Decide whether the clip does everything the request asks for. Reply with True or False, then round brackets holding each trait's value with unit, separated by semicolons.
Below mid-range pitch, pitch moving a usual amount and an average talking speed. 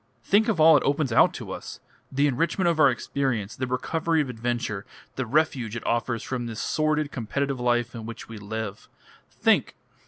True (125 Hz; 4.7 semitones; 185 wpm)